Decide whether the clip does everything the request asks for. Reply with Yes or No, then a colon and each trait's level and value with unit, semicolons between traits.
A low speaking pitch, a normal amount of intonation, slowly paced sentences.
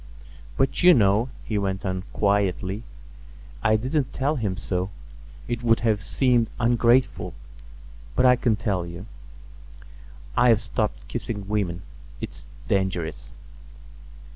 Yes: low, 105 Hz; average, 4.0 semitones; slow, 115 wpm